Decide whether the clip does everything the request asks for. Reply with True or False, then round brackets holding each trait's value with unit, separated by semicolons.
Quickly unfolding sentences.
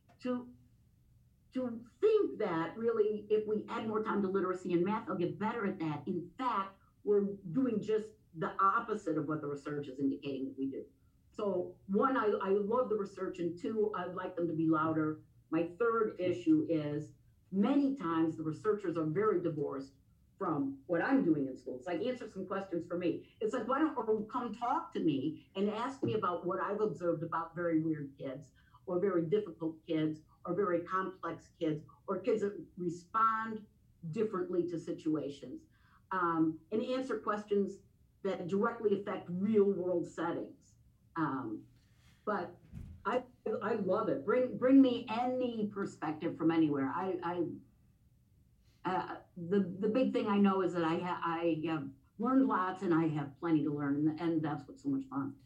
False (175 wpm)